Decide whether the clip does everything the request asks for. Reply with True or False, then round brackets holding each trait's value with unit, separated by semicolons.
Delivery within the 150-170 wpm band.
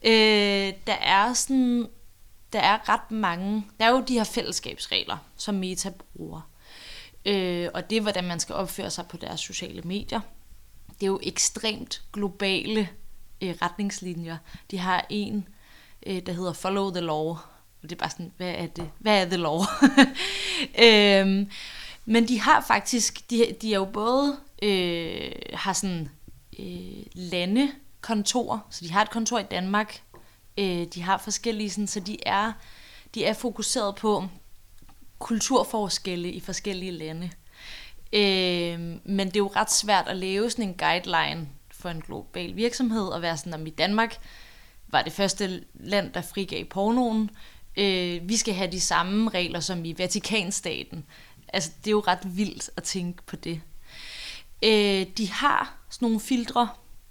True (160 wpm)